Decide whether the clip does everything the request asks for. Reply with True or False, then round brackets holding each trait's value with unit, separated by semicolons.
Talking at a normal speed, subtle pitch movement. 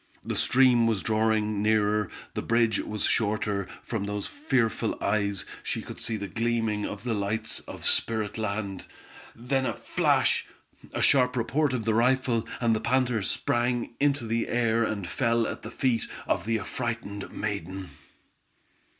True (155 wpm; 2.3 semitones)